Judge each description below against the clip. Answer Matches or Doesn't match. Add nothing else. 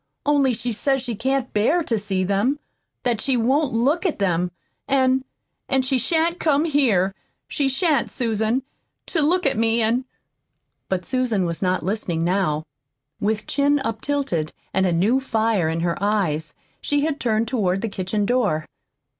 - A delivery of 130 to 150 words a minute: Doesn't match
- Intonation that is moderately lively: Doesn't match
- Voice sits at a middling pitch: Doesn't match